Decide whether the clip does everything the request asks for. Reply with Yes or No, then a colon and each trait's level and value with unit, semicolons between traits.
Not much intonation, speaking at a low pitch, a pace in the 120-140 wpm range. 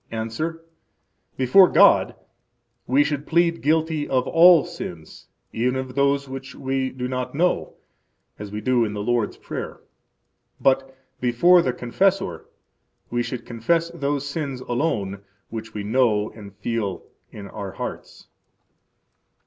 No: average, 4.8 semitones; low, 130 Hz; slow, 135 wpm